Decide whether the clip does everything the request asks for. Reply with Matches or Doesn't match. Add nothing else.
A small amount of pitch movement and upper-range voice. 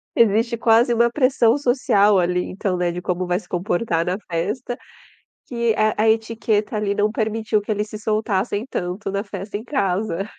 Doesn't match